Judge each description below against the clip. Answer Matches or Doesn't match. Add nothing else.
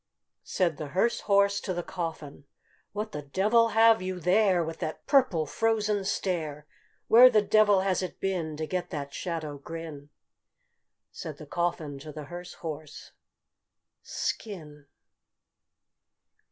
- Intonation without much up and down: Doesn't match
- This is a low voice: Doesn't match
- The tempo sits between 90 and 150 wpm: Matches